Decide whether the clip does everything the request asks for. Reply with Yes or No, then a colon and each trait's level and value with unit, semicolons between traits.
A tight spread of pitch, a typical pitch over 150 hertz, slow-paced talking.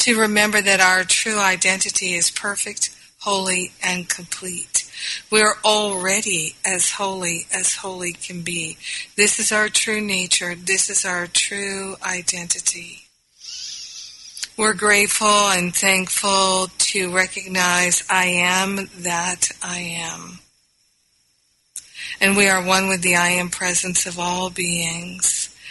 Yes: narrow, 2.1 semitones; medium, 185 Hz; slow, 125 wpm